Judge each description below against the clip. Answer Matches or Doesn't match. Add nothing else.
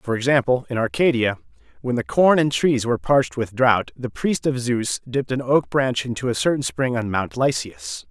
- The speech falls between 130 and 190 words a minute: Doesn't match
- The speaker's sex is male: Matches